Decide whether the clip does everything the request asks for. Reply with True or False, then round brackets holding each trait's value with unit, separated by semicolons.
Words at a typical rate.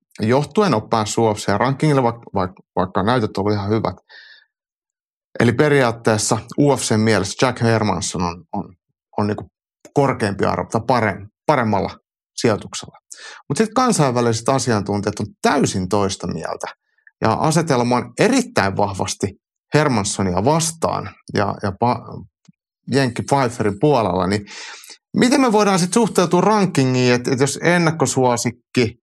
True (120 wpm)